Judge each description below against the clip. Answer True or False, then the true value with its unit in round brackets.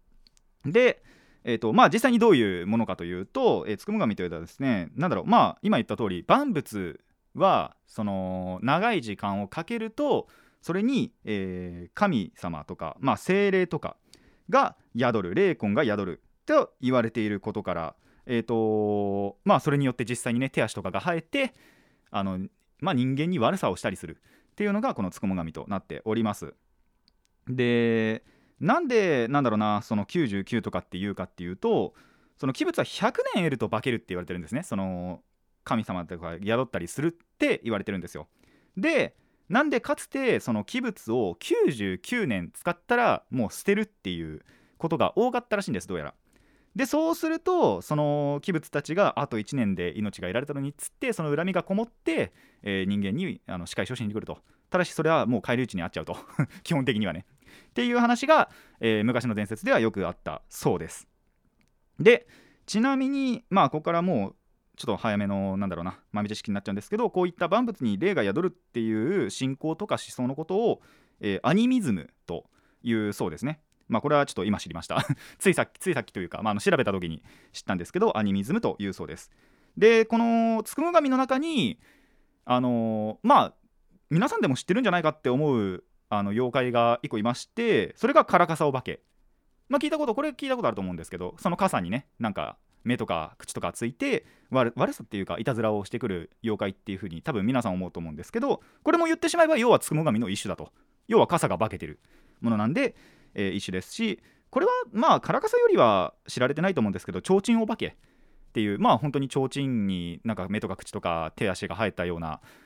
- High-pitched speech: False (125 Hz)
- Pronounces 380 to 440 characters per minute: True (390 characters per minute)